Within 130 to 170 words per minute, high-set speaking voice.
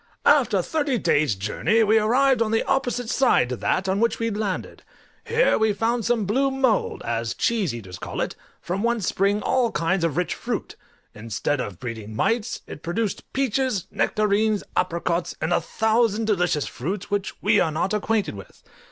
No: average, 180 wpm; high, 210 Hz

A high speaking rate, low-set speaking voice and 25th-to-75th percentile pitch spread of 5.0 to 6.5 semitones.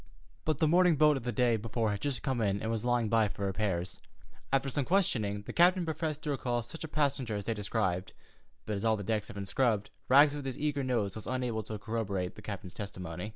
Yes: fast, 235 wpm; low, 115 Hz; average, 5.3 semitones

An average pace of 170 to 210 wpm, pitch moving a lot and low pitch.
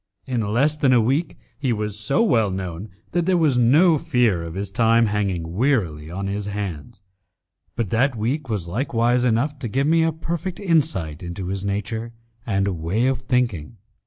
Yes: average, 180 wpm; wide, 5.7 semitones; low, 115 Hz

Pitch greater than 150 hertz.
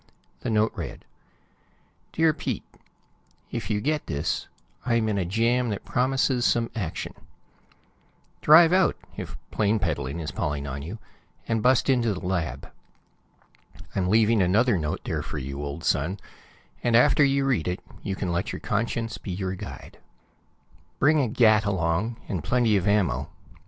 No: low, 105 Hz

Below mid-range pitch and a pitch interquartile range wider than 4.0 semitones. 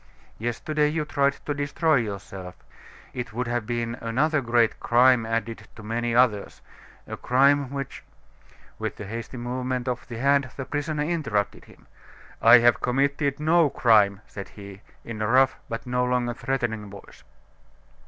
No: low, 125 Hz; average, 3.4 semitones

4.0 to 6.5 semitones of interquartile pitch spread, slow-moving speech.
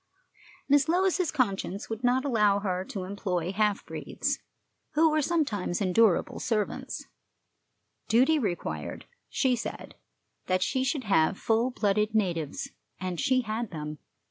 Yes: wide, 5.6 semitones; slow, 130 wpm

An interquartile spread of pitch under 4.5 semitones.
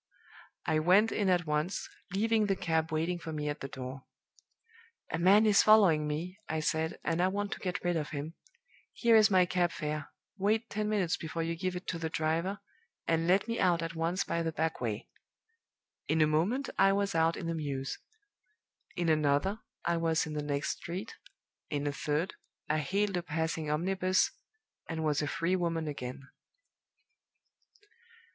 Yes: average, 3.5 semitones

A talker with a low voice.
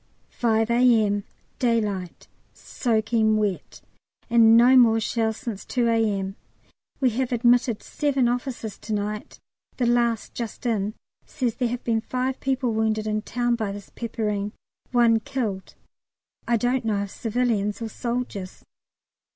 No: high, 230 Hz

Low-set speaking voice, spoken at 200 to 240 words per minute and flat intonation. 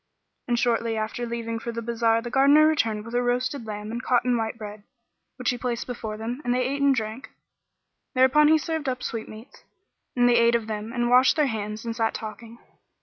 No: high, 235 Hz; fast, 205 wpm; narrow, 2.1 semitones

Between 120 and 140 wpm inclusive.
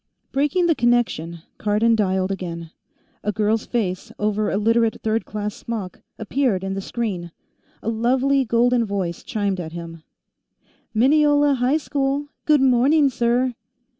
Yes: slow, 135 wpm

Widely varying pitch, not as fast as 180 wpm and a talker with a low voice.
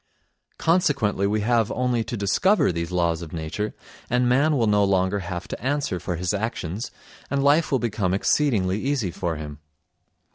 Yes: wide, 5.7 semitones; average, 170 wpm; low, 105 Hz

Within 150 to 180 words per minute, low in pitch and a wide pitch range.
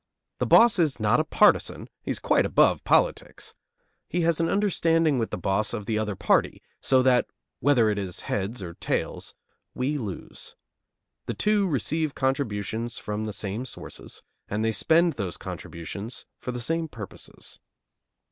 Yes: average, 160 wpm; low, 125 Hz; wide, 7.3 semitones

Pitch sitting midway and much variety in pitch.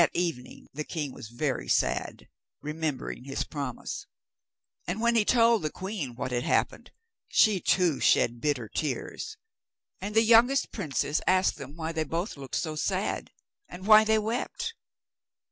Yes: medium, 165 Hz; wide, 7.2 semitones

